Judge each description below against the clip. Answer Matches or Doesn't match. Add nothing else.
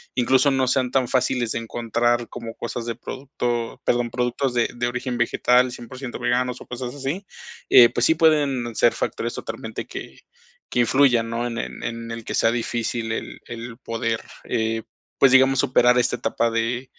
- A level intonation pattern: Matches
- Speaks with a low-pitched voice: Matches